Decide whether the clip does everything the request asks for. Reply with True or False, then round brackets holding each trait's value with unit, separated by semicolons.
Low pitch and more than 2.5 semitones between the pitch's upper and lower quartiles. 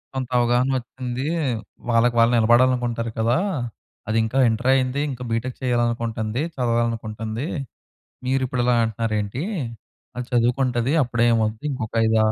False (120 Hz; 1.9 semitones)